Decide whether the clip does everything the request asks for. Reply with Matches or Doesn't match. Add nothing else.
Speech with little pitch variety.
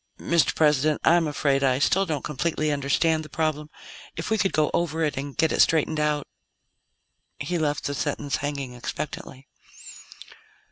Matches